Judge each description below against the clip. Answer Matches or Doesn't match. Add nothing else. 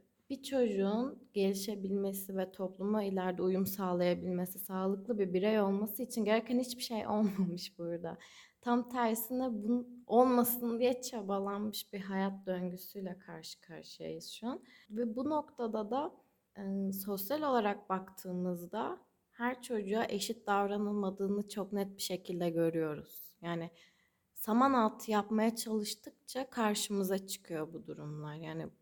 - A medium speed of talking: Matches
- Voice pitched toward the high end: Matches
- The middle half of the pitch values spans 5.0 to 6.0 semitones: Doesn't match